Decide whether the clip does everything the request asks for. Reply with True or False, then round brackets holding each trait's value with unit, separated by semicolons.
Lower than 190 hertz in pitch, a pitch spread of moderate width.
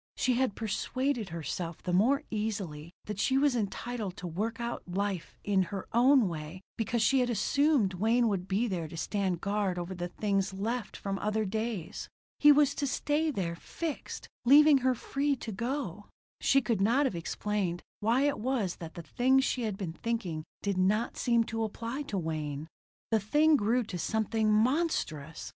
False (215 Hz; 5.0 semitones)